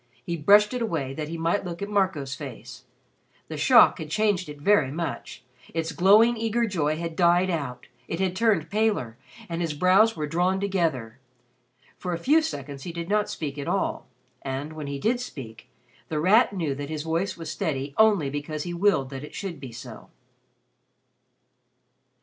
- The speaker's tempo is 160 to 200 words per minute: Yes, average, 180 wpm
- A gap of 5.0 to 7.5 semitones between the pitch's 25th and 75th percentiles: Yes, average, 5.3 semitones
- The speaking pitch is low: No, medium, 165 Hz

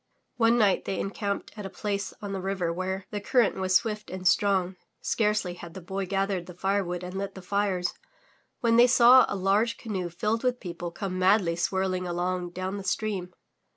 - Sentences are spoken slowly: No, average, 195 wpm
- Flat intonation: Yes, narrow, 2.1 semitones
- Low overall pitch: No, high, 195 Hz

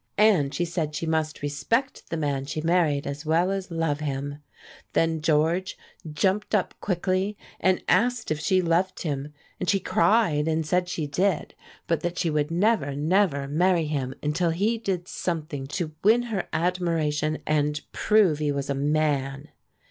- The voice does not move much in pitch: No, average, 3.9 semitones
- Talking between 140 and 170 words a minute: Yes, average, 165 wpm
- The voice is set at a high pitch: No, medium, 165 Hz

